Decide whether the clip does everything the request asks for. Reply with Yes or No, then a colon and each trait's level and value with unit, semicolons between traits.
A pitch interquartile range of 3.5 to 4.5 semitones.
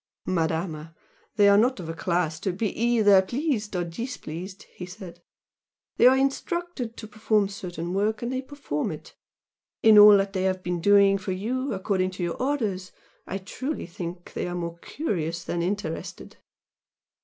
Yes: average, 4.1 semitones